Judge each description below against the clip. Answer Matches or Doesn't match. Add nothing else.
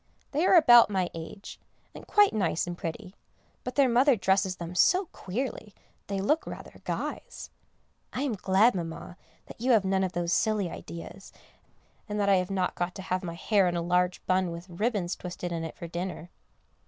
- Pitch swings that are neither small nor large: Matches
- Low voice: Doesn't match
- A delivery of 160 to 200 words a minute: Matches